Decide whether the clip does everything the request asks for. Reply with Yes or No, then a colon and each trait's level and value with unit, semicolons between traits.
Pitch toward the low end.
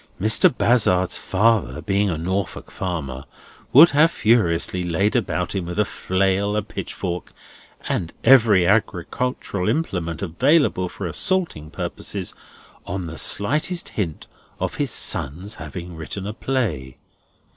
Yes: very low, 95 Hz